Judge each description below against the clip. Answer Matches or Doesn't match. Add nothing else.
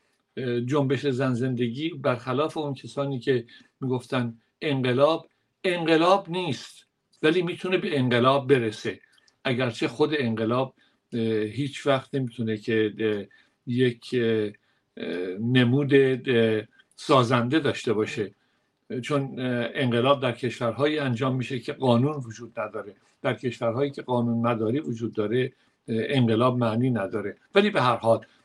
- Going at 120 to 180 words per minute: Doesn't match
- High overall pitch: Doesn't match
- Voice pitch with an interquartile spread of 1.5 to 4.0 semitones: Matches